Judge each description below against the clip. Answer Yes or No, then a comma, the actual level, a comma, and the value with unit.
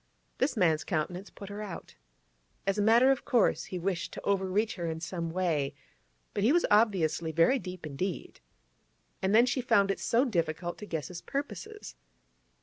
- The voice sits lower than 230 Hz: Yes, high, 190 Hz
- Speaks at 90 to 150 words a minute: No, average, 175 wpm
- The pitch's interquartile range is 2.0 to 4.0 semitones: No, average, 4.4 semitones